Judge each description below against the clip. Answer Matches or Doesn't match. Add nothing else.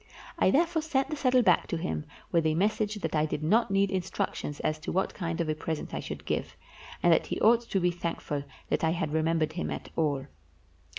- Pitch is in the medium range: Matches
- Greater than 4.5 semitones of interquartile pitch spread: Matches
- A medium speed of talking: Doesn't match